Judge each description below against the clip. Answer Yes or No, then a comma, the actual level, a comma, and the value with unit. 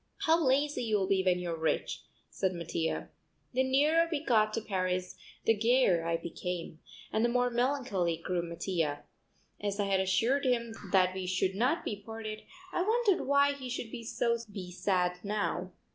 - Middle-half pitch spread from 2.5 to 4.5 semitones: No, wide, 5.6 semitones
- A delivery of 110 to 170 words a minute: Yes, average, 165 wpm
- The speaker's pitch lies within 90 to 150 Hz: No, high, 210 Hz